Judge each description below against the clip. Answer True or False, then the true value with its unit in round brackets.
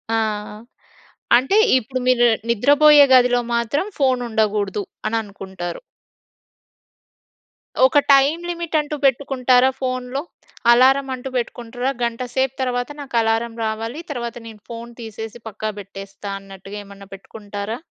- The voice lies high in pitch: True (240 Hz)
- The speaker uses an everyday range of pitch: True (3.5 semitones)